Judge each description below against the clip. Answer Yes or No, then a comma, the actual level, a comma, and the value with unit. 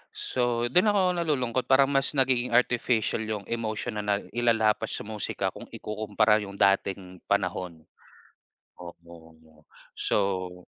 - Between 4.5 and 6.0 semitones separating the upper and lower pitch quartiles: Yes, average, 4.8 semitones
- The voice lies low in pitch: Yes, low, 110 Hz